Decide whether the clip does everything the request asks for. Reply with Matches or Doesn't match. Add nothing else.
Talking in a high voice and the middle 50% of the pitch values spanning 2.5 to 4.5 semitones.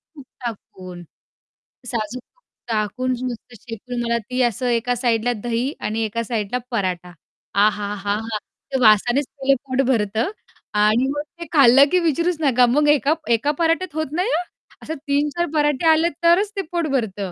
Doesn't match